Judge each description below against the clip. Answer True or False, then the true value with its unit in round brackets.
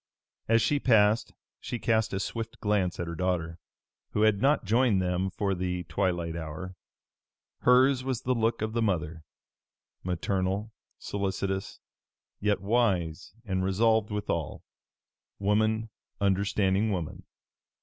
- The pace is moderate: False (125 wpm)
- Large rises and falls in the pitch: False (3.3 semitones)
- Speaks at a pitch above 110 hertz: False (100 Hz)